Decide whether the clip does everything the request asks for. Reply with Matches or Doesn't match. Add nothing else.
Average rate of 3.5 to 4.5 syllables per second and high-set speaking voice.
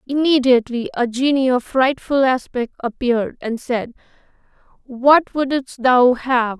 Matches